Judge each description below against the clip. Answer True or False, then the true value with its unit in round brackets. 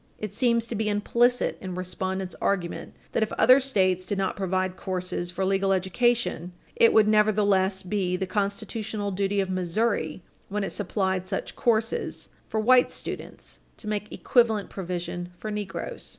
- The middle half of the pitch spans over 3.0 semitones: False (2.6 semitones)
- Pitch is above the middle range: True (200 Hz)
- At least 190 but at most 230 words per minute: False (155 wpm)